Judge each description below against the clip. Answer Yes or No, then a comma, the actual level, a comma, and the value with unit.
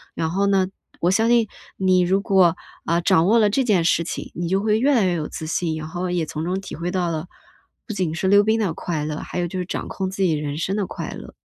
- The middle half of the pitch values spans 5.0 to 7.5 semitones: No, average, 3.0 semitones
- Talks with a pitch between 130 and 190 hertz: Yes, medium, 185 Hz